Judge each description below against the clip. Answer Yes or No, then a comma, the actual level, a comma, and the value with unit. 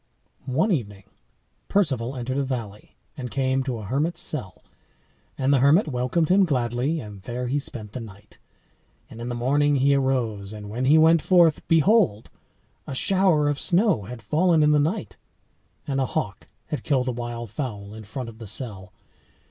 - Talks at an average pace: Yes, average, 180 wpm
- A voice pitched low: Yes, low, 130 Hz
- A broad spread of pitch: No, average, 4.8 semitones